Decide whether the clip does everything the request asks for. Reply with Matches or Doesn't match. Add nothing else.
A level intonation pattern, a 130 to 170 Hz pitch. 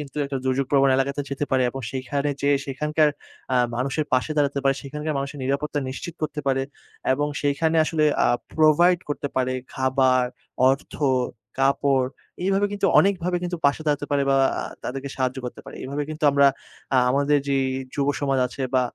Matches